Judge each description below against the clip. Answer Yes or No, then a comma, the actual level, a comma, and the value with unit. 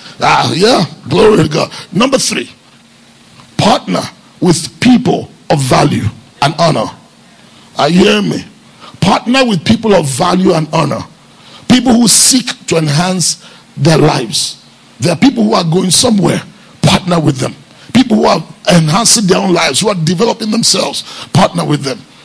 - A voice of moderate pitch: Yes, medium, 180 Hz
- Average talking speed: Yes, average, 150 wpm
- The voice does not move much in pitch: No, average, 5.2 semitones